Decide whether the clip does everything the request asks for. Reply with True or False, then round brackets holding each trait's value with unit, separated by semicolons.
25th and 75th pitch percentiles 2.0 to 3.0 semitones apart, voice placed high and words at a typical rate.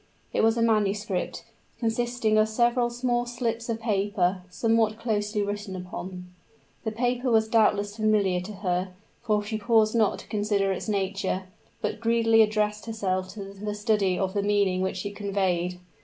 True (2.5 semitones; 210 Hz; 160 wpm)